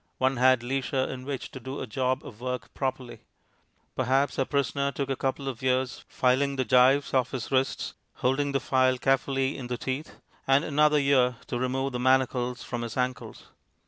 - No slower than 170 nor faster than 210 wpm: Yes, average, 185 wpm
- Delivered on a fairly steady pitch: Yes, narrow, 1.3 semitones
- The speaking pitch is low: Yes, low, 130 Hz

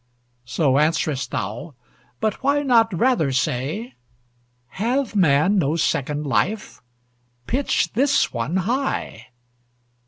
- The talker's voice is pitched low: No, medium, 175 Hz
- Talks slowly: Yes, slow, 100 wpm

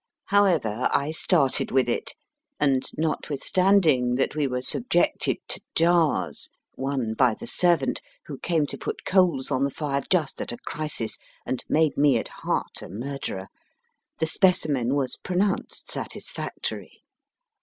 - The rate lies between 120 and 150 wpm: Yes, average, 140 wpm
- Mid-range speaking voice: Yes, medium, 145 Hz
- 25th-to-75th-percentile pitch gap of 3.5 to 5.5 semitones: Yes, average, 4.6 semitones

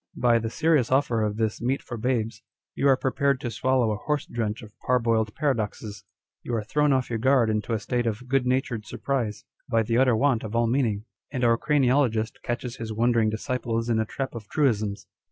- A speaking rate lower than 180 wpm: No, fast, 205 wpm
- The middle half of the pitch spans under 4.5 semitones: Yes, average, 2.8 semitones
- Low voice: Yes, low, 115 Hz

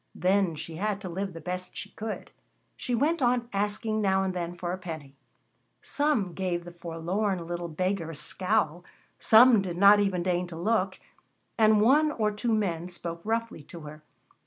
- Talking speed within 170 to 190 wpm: Yes, average, 180 wpm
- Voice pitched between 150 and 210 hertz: Yes, high, 190 Hz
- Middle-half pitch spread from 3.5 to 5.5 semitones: Yes, average, 3.8 semitones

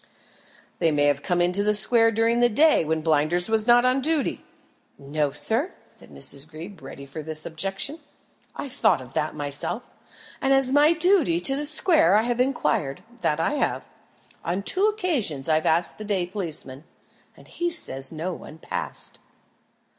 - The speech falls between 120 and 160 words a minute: No, average, 170 wpm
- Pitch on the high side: Yes, high, 195 Hz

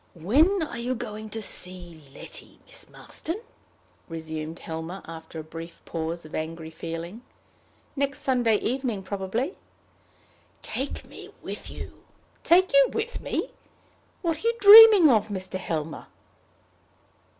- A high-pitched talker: Yes, high, 205 Hz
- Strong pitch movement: Yes, wide, 9.0 semitones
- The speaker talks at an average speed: No, slow, 130 wpm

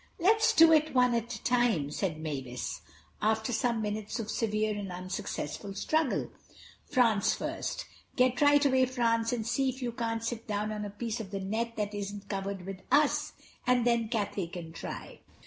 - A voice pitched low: No, high, 220 Hz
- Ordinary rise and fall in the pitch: Yes, average, 3.5 semitones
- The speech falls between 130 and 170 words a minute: No, average, 180 wpm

